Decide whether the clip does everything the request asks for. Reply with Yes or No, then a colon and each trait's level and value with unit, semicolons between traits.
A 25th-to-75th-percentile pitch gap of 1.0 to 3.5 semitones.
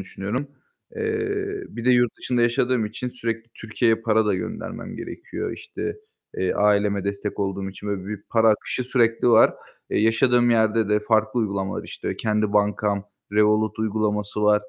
Yes: narrow, 2.4 semitones